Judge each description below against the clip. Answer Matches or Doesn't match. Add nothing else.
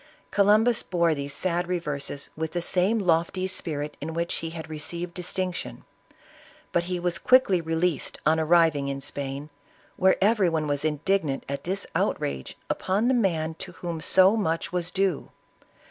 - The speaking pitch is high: Doesn't match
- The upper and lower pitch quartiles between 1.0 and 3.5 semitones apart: Matches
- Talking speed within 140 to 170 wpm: Matches